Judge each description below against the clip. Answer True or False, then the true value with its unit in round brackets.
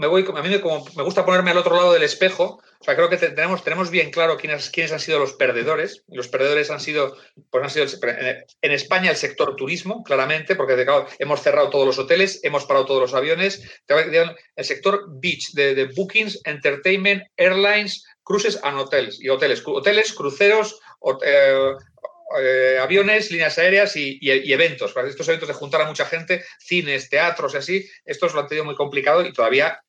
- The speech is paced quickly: True (200 wpm)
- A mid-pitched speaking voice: True (180 Hz)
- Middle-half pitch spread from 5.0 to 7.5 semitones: True (5.6 semitones)